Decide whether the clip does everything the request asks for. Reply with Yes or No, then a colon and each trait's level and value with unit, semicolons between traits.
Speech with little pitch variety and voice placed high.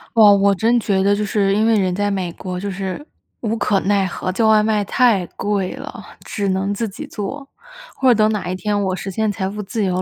Yes: narrow, 2.2 semitones; high, 205 Hz